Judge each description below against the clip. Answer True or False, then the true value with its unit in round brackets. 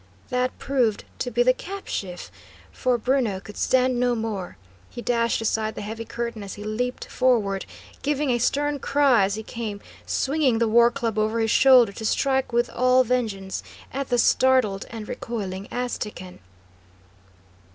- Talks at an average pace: True (160 wpm)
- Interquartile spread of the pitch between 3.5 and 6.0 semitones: False (2.9 semitones)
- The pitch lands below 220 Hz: False (235 Hz)